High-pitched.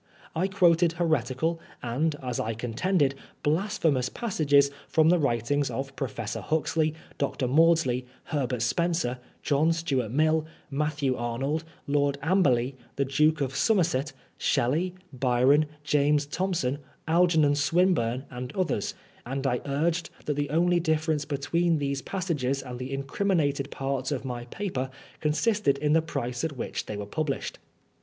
No: medium, 145 Hz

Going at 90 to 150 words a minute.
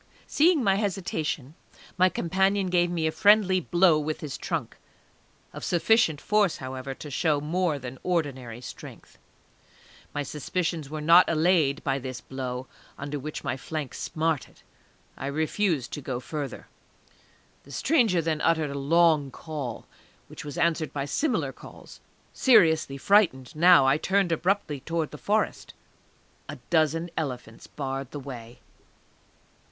Yes: average, 140 wpm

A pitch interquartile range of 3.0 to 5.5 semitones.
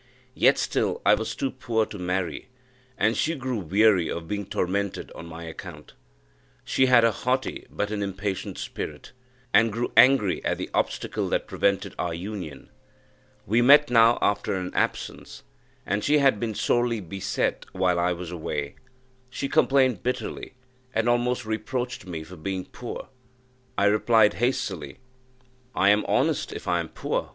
Yes: average, 4.8 semitones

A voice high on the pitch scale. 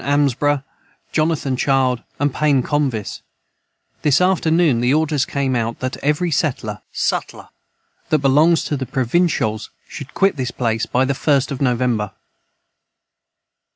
No: medium, 140 Hz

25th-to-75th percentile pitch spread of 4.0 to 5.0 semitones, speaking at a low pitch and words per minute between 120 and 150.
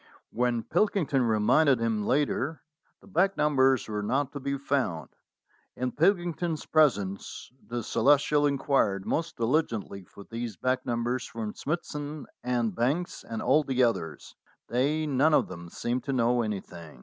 Yes: average, 4.6 semitones; low, 130 Hz; average, 145 wpm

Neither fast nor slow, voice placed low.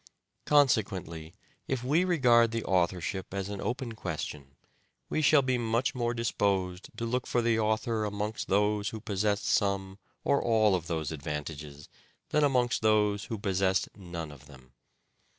Yes: average, 150 wpm; low, 105 Hz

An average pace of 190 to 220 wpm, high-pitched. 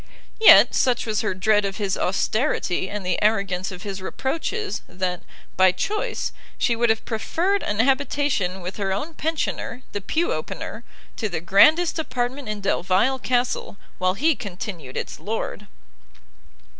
No: average, 150 wpm; high, 215 Hz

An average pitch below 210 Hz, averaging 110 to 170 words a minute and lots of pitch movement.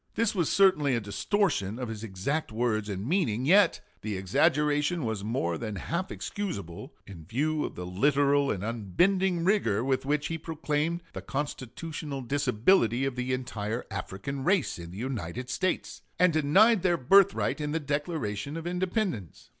Yes: medium, 140 Hz; average, 160 wpm; wide, 7.5 semitones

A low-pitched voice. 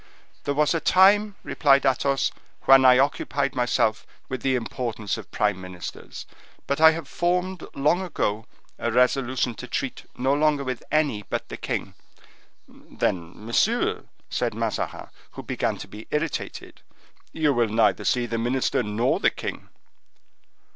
Yes: low, 130 Hz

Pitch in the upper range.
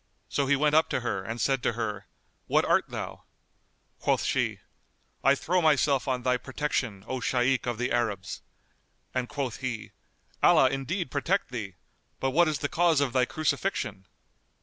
No: low, 130 Hz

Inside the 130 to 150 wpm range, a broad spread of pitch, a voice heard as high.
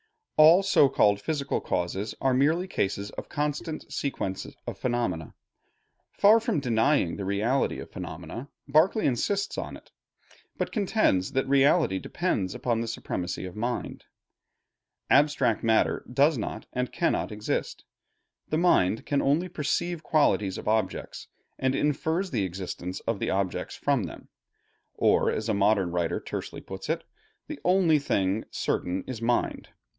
No: average, 145 wpm; wide, 7.4 semitones; low, 125 Hz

